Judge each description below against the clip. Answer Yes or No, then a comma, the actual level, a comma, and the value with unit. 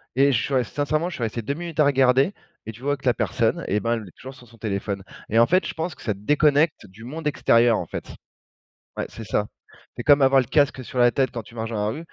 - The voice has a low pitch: Yes, low, 130 Hz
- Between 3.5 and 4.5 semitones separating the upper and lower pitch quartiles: Yes, average, 4.2 semitones